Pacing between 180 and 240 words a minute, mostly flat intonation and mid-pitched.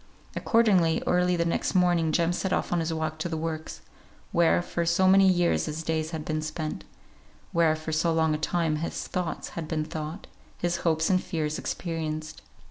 Yes: average, 190 wpm; narrow, 1.8 semitones; medium, 165 Hz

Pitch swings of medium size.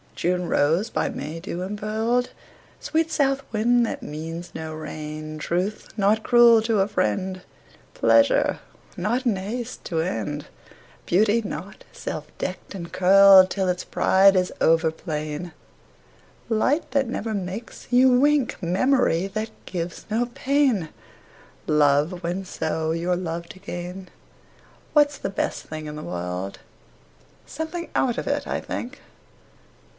No: wide, 5.9 semitones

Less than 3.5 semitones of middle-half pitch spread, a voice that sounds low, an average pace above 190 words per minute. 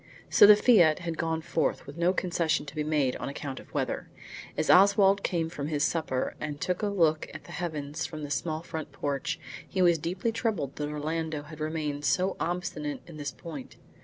No: average, 2.9 semitones; medium, 160 Hz; average, 200 wpm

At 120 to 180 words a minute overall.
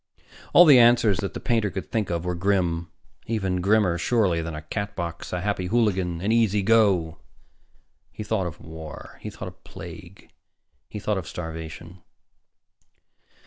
Yes: average, 155 wpm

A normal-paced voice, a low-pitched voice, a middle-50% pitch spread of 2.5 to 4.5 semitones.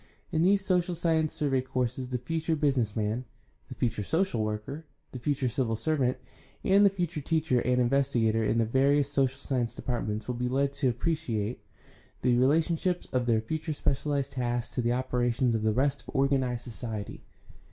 Yes: average, 175 wpm; low, 130 Hz; average, 3.9 semitones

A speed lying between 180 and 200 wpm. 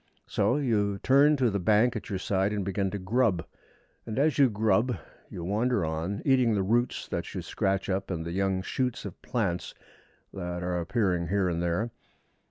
Yes: average, 185 wpm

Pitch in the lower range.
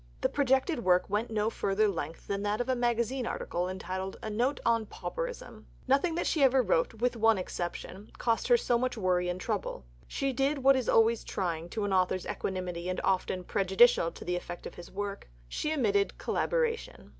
No: high, 220 Hz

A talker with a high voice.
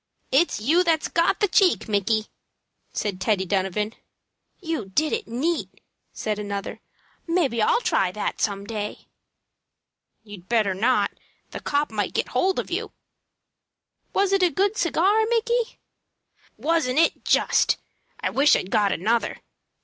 Yes: very high, 250 Hz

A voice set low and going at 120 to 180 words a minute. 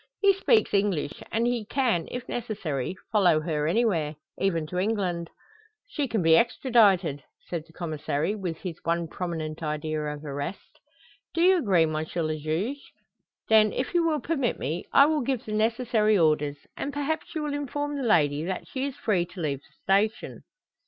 No: high, 195 Hz; average, 175 wpm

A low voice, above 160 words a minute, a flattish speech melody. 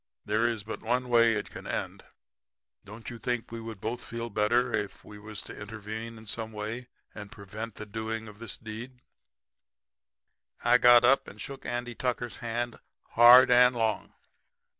Yes: low, 115 Hz; average, 170 wpm; narrow, 2.0 semitones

